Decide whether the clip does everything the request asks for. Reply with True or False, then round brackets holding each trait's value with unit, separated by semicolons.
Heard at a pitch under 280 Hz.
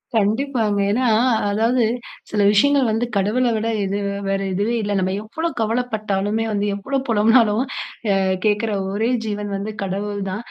True (215 Hz)